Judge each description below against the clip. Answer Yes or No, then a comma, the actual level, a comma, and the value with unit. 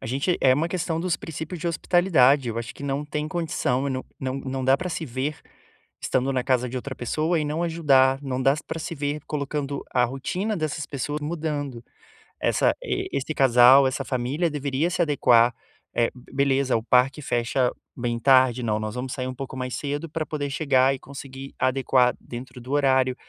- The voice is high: No, low, 135 Hz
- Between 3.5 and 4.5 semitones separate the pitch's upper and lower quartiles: No, average, 2.8 semitones